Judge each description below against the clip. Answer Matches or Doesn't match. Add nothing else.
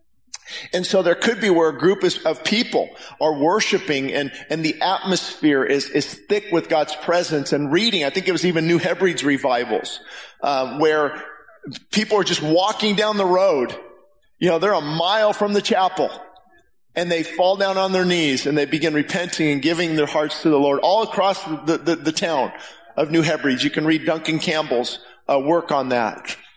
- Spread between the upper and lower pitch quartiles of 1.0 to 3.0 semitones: Doesn't match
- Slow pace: Doesn't match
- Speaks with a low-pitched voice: Doesn't match